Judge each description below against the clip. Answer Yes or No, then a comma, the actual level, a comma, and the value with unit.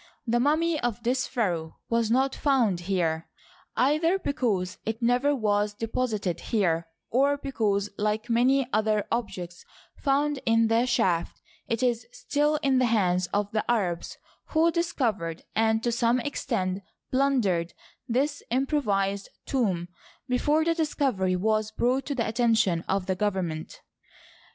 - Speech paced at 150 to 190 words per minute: No, slow, 135 wpm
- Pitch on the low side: No, high, 230 Hz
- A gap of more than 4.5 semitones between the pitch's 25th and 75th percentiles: Yes, average, 5.1 semitones